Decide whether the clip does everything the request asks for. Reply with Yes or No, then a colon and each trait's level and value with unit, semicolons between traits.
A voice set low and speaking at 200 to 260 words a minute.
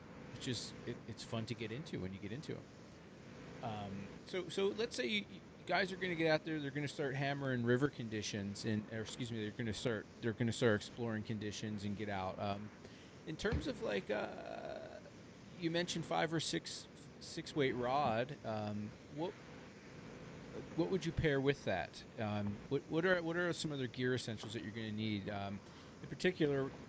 Yes: low, 120 Hz; fast, 205 wpm